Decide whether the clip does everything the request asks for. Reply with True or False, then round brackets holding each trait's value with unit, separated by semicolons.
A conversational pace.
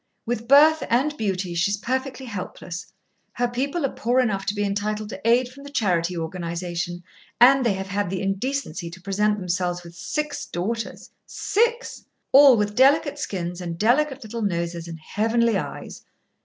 True (170 wpm)